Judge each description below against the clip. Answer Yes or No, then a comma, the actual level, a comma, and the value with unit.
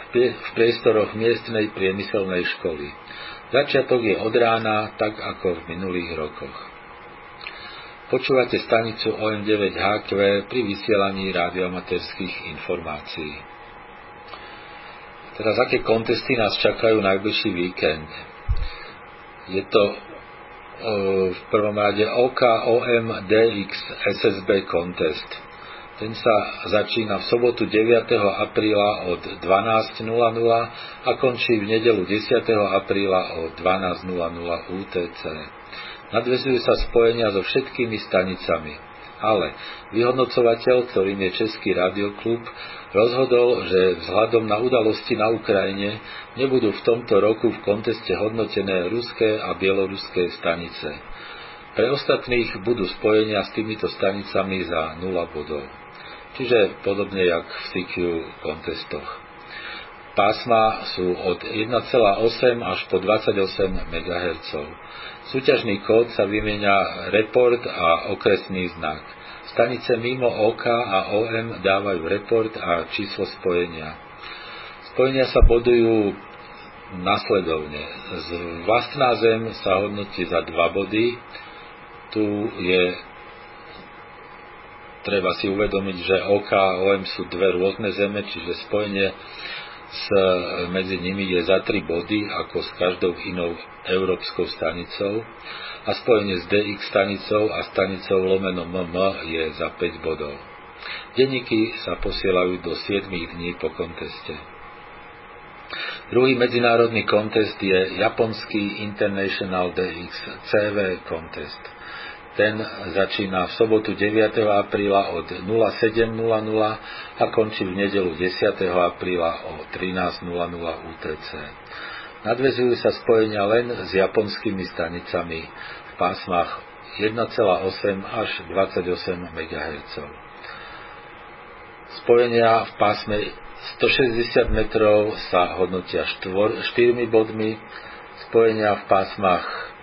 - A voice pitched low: Yes, low, 100 Hz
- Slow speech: Yes, slow, 105 wpm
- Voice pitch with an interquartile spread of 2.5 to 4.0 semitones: Yes, average, 3.5 semitones